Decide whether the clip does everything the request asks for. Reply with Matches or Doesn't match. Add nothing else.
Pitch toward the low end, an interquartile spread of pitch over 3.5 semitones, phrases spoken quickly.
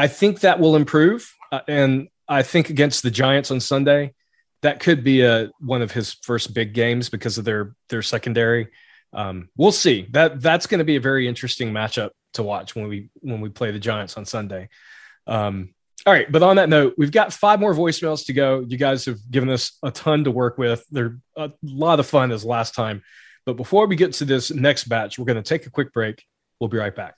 Matches